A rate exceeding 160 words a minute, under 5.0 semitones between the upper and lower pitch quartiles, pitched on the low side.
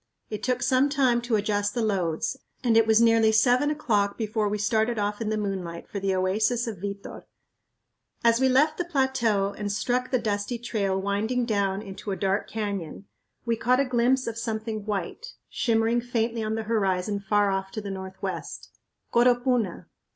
No: average, 180 wpm; average, 3.1 semitones; high, 220 Hz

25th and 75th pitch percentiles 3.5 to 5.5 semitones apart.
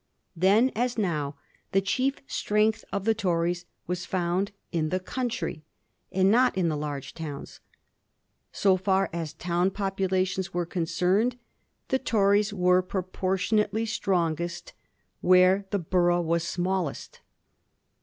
No: average, 2.7 semitones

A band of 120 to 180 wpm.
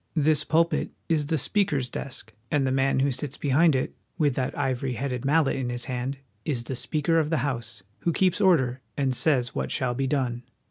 No: average, 200 wpm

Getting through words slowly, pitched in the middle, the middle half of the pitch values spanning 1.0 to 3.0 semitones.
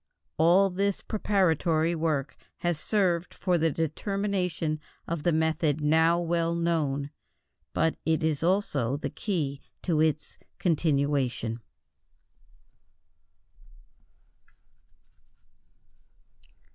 Yes: slow, 85 wpm; medium, 160 Hz; narrow, 2.5 semitones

